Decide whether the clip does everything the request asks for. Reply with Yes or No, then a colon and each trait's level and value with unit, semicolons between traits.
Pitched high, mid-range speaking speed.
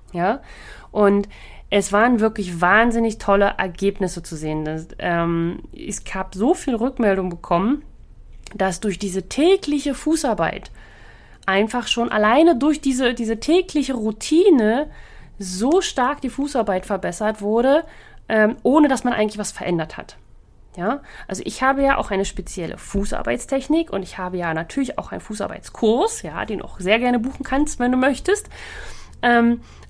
Yes: high, 220 Hz; average, 150 wpm